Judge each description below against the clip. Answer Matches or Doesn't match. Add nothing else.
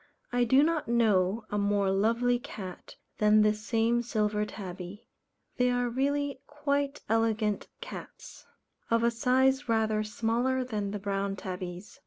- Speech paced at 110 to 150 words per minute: Matches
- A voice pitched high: Matches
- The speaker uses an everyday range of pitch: Matches